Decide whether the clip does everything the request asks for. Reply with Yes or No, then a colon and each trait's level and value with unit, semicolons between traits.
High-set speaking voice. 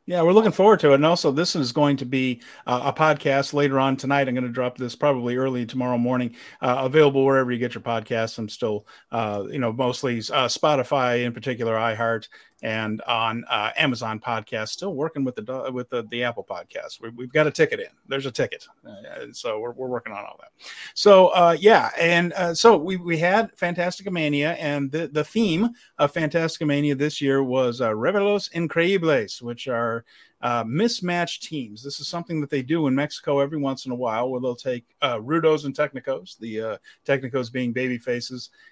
No: low, 135 Hz